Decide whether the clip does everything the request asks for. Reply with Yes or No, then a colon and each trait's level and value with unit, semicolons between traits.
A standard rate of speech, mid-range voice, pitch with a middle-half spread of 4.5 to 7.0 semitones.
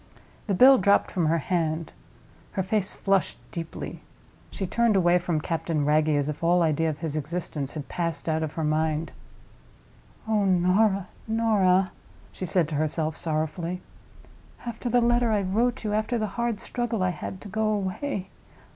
Yes: average, 165 wpm; medium, 180 Hz; average, 5.0 semitones